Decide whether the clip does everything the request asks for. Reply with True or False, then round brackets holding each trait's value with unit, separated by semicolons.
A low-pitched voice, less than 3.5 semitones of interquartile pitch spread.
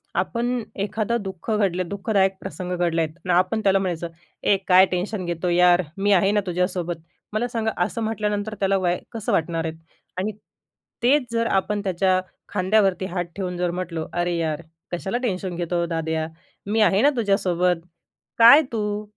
False (190 Hz; 3.1 semitones)